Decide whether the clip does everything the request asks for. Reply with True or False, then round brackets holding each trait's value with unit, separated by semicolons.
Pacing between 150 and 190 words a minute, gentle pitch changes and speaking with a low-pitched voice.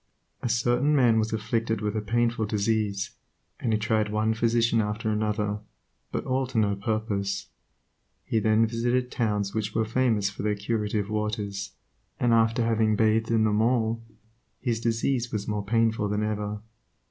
True (160 wpm; 1.6 semitones; 110 Hz)